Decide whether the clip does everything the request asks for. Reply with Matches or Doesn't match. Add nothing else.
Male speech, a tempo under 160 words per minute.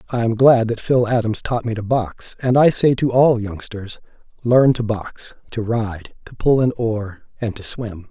Doesn't match